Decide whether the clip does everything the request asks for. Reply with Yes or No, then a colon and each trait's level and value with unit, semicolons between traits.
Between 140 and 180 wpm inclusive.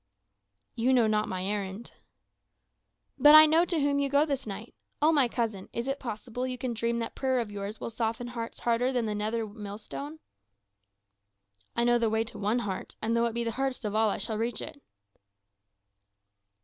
No: average, 195 wpm